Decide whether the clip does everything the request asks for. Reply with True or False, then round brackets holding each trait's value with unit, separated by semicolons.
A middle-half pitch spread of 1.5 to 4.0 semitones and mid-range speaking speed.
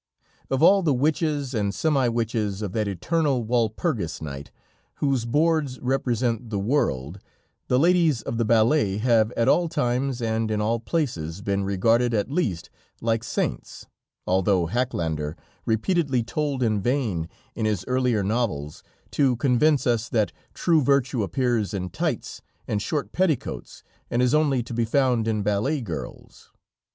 False (4.7 semitones; 150 wpm)